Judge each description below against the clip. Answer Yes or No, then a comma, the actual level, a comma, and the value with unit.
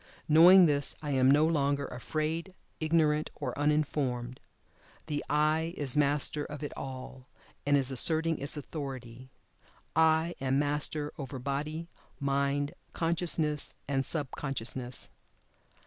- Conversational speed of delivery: No, slow, 120 wpm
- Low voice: No, medium, 145 Hz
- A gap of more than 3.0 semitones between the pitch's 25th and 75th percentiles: No, narrow, 2.5 semitones